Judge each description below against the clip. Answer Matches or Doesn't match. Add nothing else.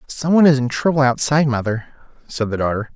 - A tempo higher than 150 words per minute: Matches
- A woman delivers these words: Doesn't match